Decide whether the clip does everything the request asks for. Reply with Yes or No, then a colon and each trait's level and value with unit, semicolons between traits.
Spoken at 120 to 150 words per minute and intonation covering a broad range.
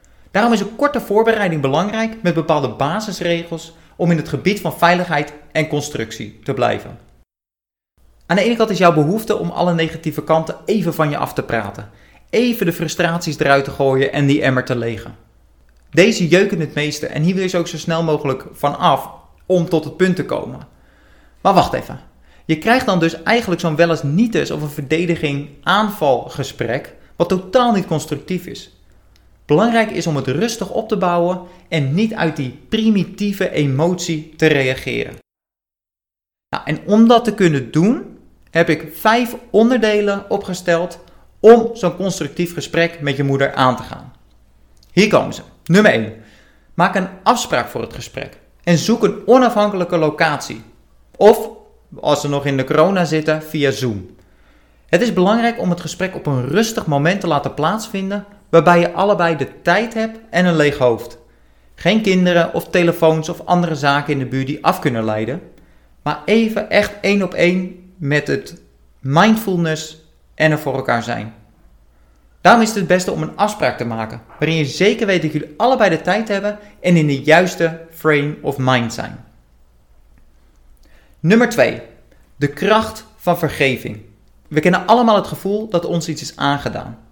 No: average, 170 wpm; wide, 5.9 semitones